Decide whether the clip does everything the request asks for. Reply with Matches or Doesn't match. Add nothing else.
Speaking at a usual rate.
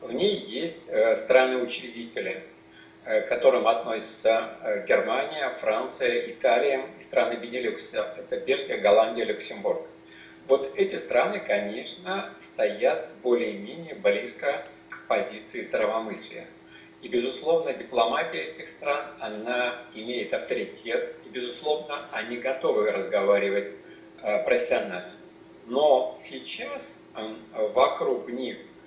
Doesn't match